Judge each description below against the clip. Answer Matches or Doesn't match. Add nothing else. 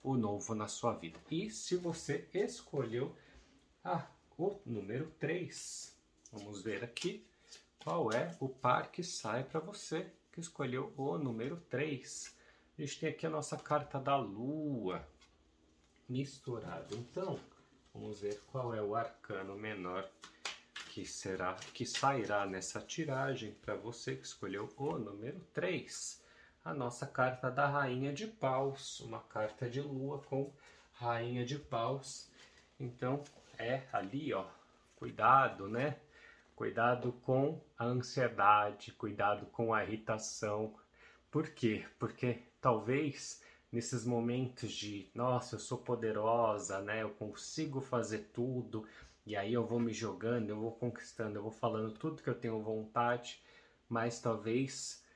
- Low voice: Matches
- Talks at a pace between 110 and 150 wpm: Matches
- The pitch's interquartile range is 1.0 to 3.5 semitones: Doesn't match